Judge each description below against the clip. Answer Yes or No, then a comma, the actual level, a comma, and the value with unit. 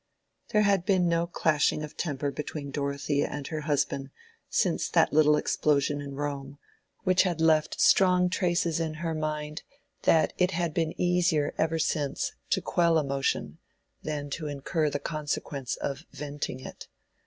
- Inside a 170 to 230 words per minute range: No, average, 155 wpm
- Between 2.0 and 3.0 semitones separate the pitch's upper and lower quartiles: Yes, average, 2.7 semitones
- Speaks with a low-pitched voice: No, medium, 155 Hz